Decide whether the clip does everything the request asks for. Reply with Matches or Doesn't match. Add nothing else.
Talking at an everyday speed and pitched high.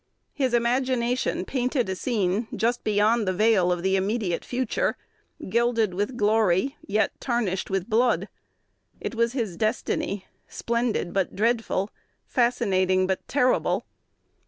Doesn't match